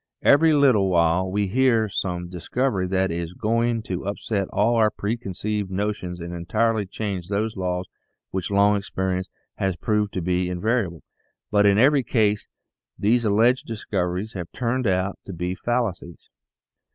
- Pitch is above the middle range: No, low, 100 Hz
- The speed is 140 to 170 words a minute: Yes, average, 155 wpm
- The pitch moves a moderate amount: Yes, average, 3.5 semitones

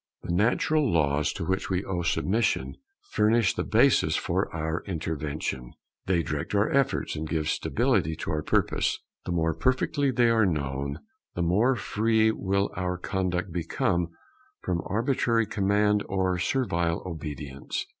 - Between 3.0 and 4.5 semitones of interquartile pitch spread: No, average, 5.0 semitones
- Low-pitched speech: Yes, very low, 90 Hz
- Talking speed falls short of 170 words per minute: Yes, average, 145 wpm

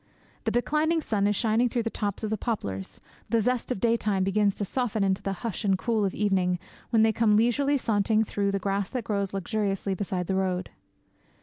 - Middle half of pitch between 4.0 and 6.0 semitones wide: No, average, 2.9 semitones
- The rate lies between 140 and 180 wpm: No, fast, 205 wpm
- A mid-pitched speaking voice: No, high, 210 Hz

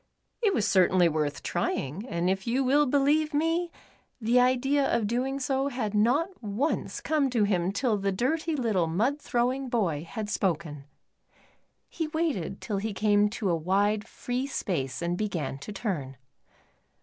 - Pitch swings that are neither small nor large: No, wide, 6.4 semitones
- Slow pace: No, average, 160 wpm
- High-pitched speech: Yes, high, 220 Hz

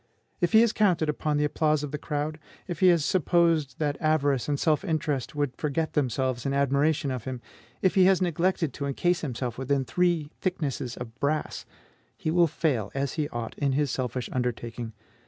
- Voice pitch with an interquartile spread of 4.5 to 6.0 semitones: No, average, 3.7 semitones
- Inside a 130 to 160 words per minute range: No, average, 190 wpm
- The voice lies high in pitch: No, medium, 145 Hz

